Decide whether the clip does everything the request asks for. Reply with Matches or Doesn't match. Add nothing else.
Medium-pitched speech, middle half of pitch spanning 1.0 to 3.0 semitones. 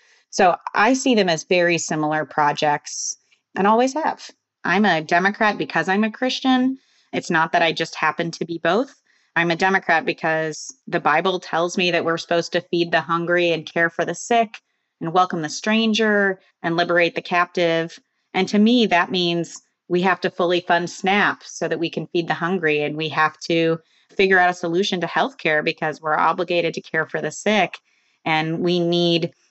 Matches